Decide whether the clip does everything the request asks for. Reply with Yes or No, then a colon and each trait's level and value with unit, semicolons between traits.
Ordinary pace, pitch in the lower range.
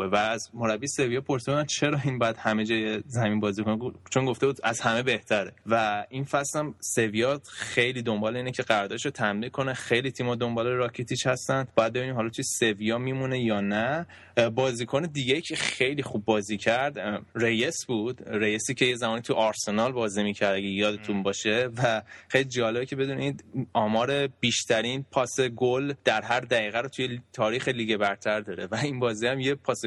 No: fast, 175 wpm; low, 120 Hz